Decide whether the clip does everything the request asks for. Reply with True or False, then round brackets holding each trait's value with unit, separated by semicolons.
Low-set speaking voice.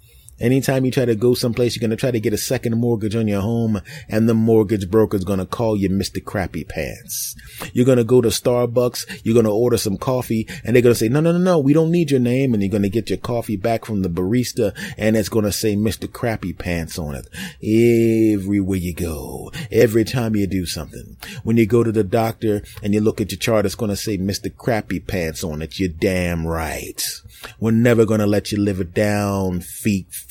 True (110 Hz)